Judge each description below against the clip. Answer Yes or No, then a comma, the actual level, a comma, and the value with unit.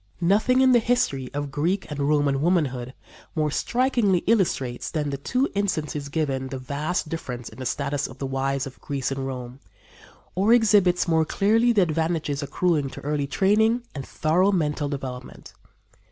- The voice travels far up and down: Yes, wide, 5.8 semitones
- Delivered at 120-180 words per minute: Yes, average, 165 wpm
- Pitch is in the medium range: Yes, medium, 150 Hz